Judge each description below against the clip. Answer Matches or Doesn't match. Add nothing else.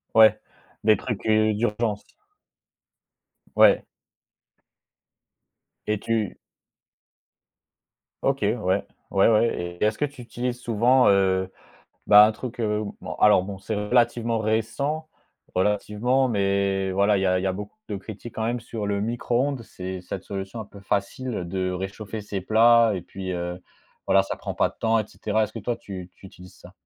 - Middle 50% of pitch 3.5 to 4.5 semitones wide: Doesn't match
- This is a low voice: Matches